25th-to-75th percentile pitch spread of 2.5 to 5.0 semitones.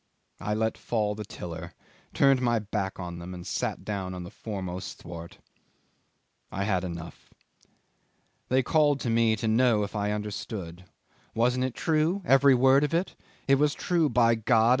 No: wide, 5.4 semitones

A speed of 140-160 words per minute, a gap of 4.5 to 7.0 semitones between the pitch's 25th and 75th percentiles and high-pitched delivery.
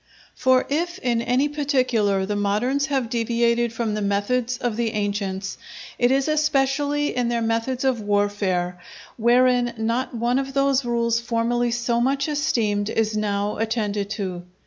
No: average, 150 wpm; average, 3.6 semitones; high, 235 Hz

